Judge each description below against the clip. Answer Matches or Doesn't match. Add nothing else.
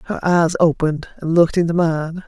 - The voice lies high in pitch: Doesn't match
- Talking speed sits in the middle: Matches